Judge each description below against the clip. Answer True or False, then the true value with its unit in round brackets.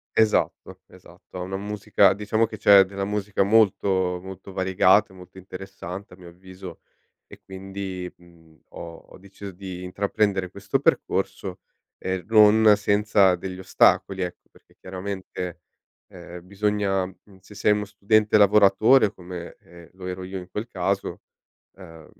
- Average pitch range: False (1.9 semitones)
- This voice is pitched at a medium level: False (95 Hz)